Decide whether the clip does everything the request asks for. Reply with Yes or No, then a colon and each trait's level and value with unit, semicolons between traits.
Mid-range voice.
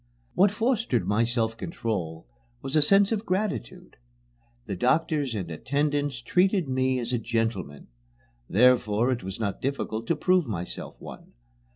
No: low, 125 Hz